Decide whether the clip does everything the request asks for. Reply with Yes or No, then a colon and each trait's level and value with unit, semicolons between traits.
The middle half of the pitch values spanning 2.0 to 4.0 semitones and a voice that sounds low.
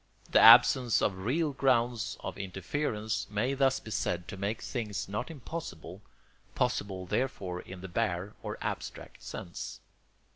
No: average, 4.8 semitones; low, 105 Hz